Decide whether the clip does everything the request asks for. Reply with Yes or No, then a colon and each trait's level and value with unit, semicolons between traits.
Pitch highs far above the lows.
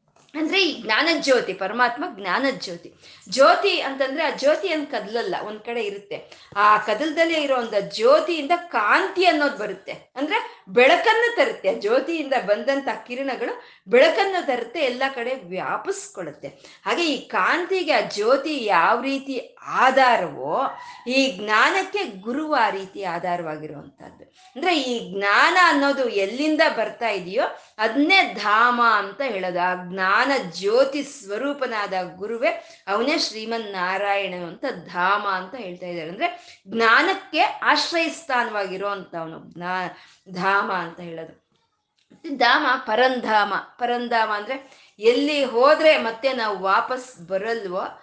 Yes: wide, 7.5 semitones